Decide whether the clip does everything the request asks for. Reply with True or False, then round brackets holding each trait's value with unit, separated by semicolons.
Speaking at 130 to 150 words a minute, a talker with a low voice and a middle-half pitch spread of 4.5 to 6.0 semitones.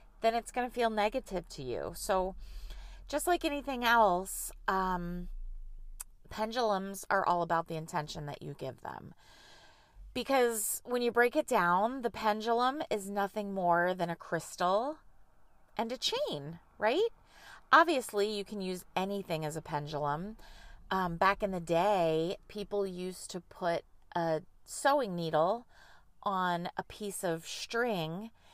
False (140 wpm; 195 Hz; 4.9 semitones)